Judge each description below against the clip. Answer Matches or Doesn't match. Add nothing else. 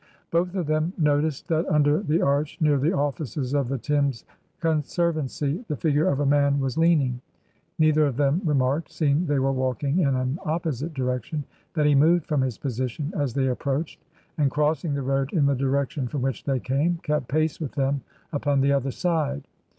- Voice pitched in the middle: Matches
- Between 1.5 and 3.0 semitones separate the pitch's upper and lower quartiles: Matches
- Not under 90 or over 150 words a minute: Doesn't match